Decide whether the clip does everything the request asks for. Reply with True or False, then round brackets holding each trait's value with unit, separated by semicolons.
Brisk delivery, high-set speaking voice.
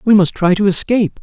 True (245 wpm; 200 Hz)